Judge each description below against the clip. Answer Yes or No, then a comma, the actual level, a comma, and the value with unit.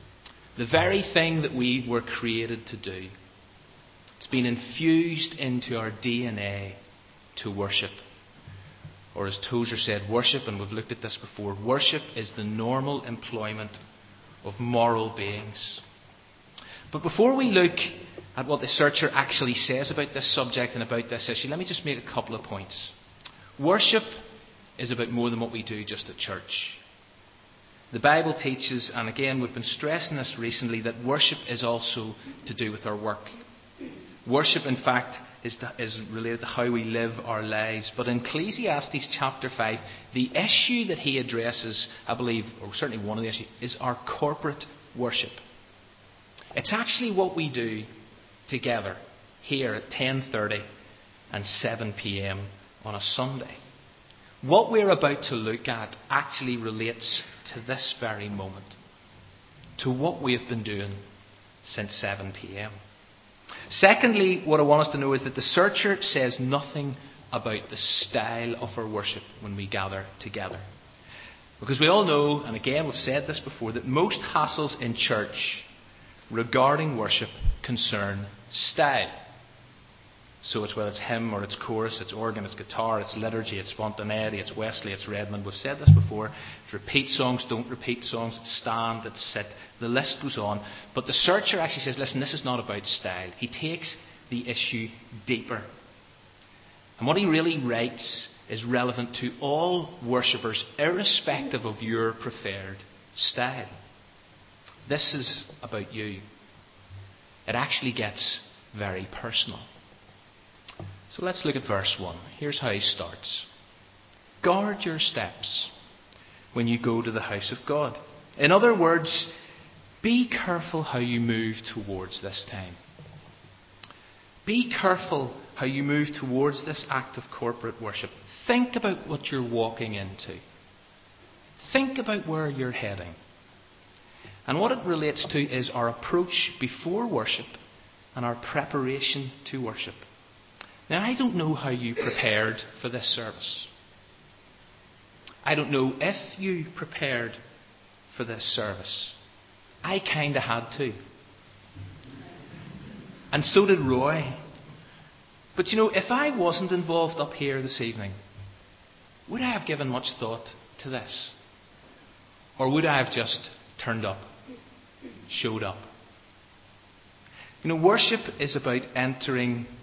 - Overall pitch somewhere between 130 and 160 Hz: No, low, 120 Hz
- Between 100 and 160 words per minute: Yes, average, 145 wpm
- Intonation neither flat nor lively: Yes, average, 4.9 semitones